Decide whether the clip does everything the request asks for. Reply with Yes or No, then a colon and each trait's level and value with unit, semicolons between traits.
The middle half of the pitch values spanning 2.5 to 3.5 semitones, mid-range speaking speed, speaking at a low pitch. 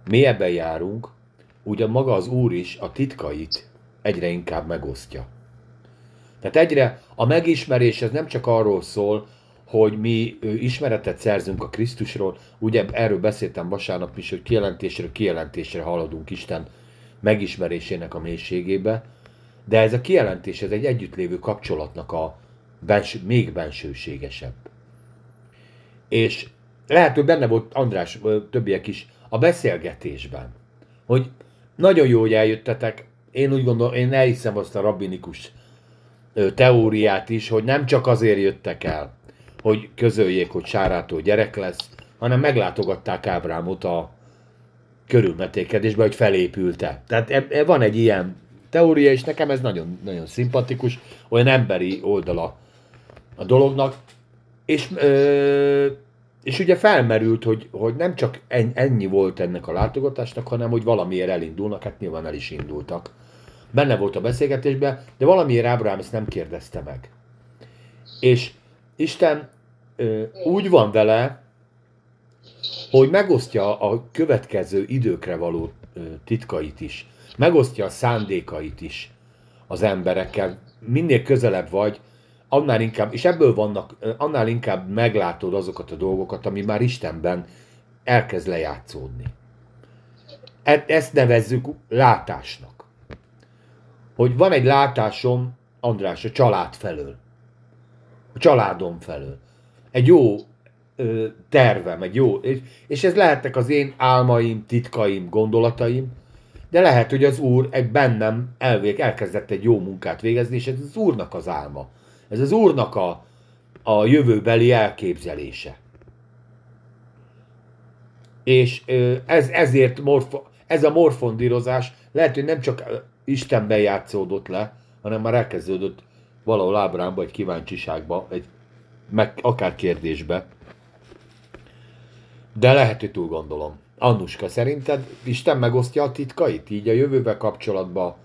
Yes: average, 3.1 semitones; average, 120 wpm; low, 120 Hz